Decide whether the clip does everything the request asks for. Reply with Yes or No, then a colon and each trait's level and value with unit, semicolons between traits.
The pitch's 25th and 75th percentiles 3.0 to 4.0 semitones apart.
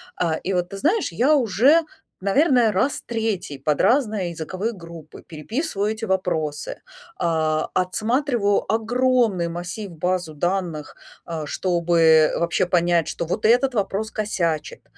No: average, 5.0 semitones